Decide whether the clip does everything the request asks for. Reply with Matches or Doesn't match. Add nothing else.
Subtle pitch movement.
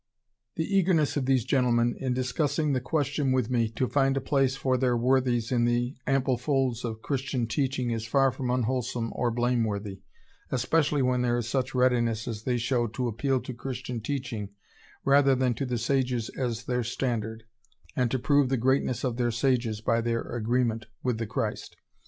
Matches